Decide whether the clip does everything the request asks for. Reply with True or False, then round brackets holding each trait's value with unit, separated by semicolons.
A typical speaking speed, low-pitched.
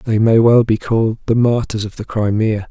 False (220 wpm; 110 Hz)